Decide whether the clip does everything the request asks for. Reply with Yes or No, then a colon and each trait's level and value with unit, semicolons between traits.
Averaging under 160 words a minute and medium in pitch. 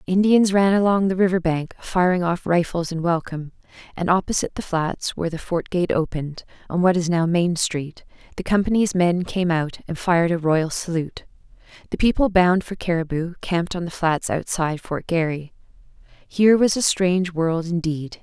No: average, 180 wpm; medium, 175 Hz